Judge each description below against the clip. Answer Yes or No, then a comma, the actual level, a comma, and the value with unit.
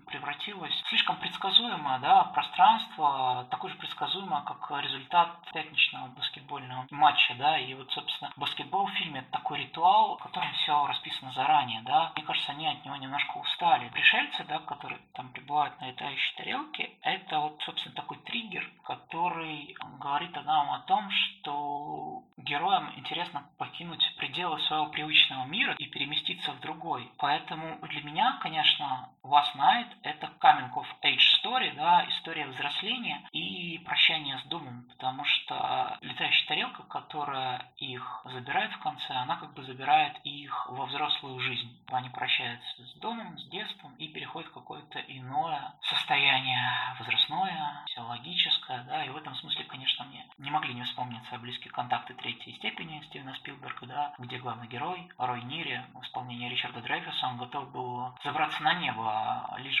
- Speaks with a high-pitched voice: No, medium, 145 Hz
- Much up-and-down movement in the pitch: No, average, 3.8 semitones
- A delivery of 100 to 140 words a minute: No, average, 150 wpm